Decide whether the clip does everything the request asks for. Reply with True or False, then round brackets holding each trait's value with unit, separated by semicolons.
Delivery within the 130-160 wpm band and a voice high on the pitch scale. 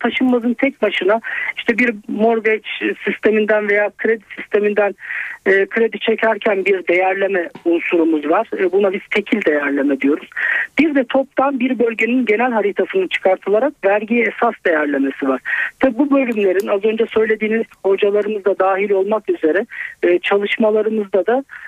True (135 wpm; 215 Hz)